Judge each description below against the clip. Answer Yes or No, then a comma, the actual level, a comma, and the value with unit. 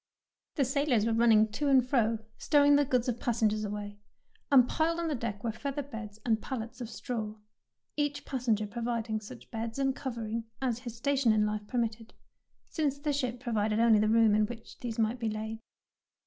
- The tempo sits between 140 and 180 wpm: No, average, 195 wpm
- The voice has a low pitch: No, high, 230 Hz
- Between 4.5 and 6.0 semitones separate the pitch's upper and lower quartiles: No, average, 3.4 semitones